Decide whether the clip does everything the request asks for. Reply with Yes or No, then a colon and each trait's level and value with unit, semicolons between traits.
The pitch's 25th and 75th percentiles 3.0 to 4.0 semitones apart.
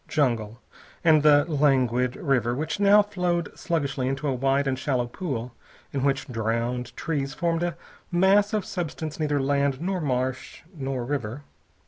No: average, 4.4 semitones